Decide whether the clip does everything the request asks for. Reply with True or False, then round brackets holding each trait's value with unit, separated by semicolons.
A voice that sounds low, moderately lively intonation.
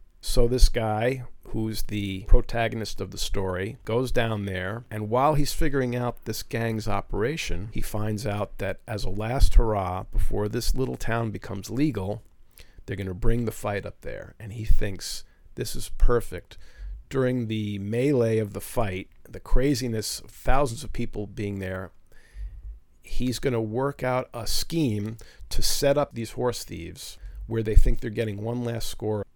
True (110 Hz; 3.3 semitones)